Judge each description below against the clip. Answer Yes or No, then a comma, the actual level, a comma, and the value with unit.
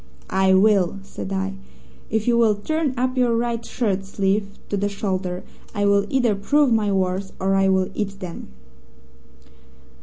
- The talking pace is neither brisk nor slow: Yes, average, 160 wpm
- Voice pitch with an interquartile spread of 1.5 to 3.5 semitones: Yes, average, 3.2 semitones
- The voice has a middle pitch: No, high, 200 Hz